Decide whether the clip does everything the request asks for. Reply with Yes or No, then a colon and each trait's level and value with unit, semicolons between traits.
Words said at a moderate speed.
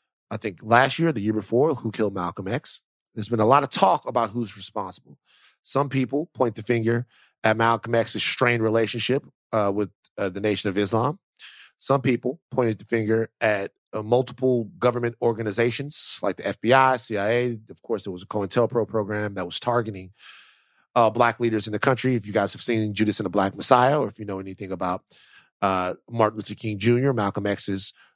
Yes: average, 190 wpm